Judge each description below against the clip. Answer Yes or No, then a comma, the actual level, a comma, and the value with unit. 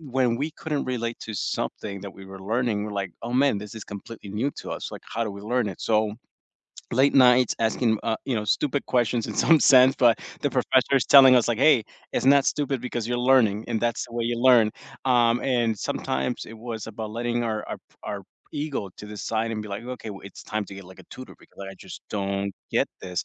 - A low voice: Yes, low, 115 Hz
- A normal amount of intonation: Yes, average, 3.2 semitones